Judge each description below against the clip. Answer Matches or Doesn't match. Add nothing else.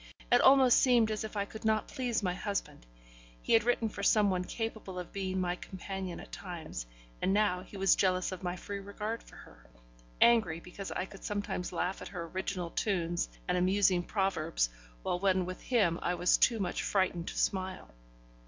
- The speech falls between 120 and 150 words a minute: Doesn't match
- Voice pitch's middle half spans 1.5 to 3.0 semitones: Matches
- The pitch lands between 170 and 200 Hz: Matches